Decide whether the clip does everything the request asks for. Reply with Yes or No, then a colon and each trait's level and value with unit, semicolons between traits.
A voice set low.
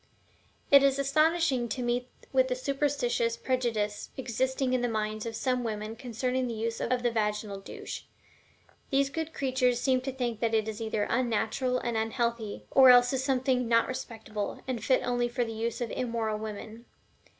No: high, 245 Hz